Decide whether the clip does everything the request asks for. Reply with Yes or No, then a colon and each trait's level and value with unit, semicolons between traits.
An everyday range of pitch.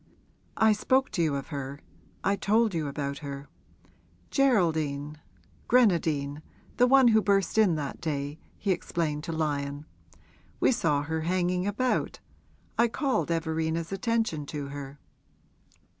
No: wide, 6.0 semitones